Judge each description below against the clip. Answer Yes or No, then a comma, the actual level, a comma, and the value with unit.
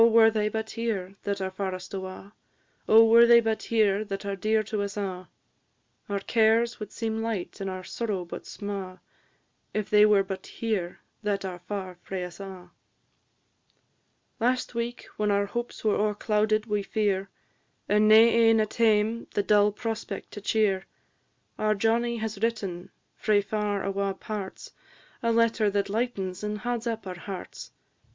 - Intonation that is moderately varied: No, narrow, 2.2 semitones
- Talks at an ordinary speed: Yes, average, 165 wpm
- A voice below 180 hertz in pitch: No, high, 210 Hz